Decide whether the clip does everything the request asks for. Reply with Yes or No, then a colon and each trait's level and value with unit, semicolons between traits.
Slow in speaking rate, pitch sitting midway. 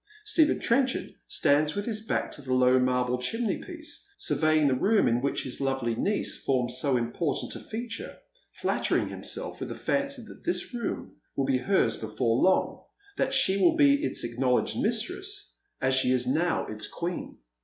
No: average, 175 wpm; medium, 155 Hz